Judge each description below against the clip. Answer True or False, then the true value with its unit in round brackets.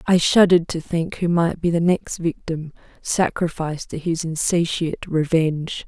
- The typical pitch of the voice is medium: True (165 Hz)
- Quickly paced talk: False (155 wpm)